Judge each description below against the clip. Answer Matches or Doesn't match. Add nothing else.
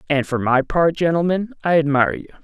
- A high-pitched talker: Doesn't match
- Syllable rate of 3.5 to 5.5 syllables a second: Doesn't match